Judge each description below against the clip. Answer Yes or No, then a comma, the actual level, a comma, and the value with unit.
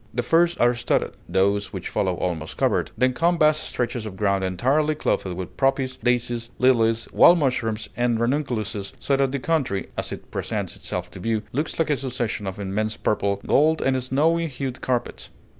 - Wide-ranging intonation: No, average, 4.5 semitones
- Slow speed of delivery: No, average, 180 wpm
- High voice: No, low, 120 Hz